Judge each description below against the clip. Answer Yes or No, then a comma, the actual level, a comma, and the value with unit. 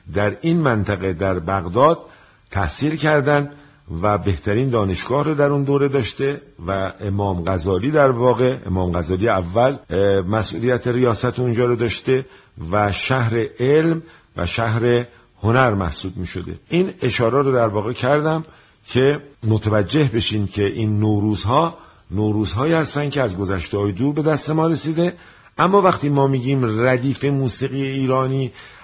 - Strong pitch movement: Yes, wide, 5.7 semitones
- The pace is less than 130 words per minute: No, average, 135 wpm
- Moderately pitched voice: No, low, 120 Hz